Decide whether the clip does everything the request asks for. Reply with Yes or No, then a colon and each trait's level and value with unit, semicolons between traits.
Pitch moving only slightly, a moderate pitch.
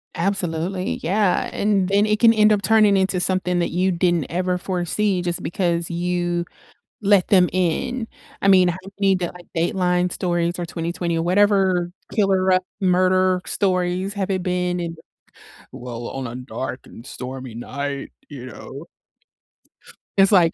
Yes: narrow, 2.2 semitones; medium, 180 Hz